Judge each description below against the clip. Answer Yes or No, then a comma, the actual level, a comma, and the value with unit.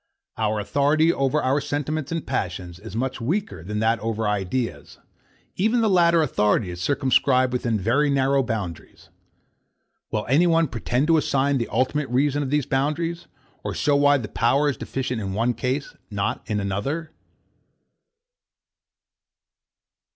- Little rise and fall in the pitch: No, average, 5.0 semitones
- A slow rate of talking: No, average, 150 wpm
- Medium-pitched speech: No, low, 130 Hz